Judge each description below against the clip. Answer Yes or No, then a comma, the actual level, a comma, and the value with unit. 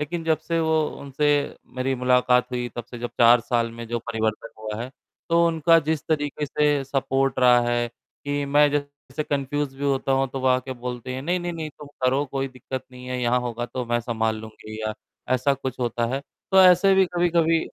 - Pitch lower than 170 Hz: Yes, low, 135 Hz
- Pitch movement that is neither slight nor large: Yes, average, 3.5 semitones